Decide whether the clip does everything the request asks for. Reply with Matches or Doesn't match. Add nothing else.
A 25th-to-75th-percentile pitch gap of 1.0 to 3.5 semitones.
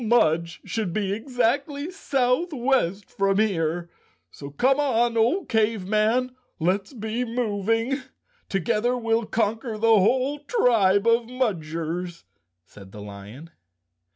Doesn't match